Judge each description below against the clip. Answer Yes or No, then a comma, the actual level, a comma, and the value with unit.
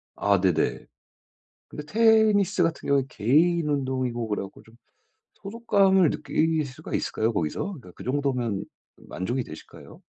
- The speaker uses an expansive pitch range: Yes, wide, 7.9 semitones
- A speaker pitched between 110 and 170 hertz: Yes, medium, 140 Hz